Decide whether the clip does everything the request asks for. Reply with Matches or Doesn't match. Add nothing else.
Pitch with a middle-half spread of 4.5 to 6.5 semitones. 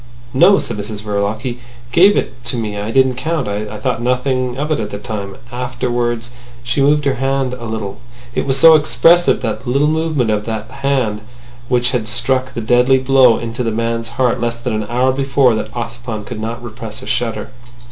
Doesn't match